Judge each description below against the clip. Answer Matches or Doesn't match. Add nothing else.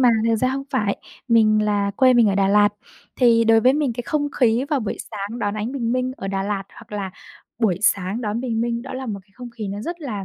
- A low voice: Doesn't match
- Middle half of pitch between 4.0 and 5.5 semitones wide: Doesn't match